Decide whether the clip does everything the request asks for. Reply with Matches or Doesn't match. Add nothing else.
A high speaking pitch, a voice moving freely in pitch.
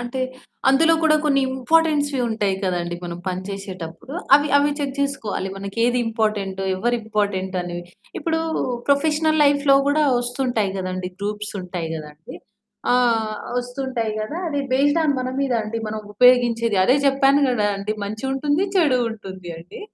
Matches